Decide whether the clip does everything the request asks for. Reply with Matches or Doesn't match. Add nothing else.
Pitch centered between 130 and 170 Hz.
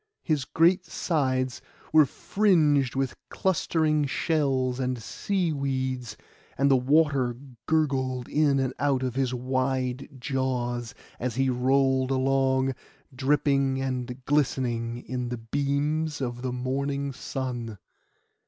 Matches